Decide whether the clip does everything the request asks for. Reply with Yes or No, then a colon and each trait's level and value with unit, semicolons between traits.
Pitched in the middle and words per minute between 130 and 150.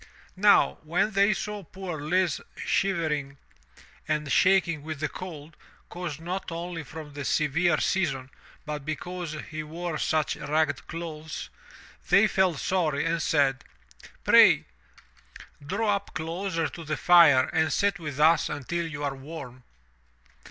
Yes: medium, 160 Hz; average, 140 wpm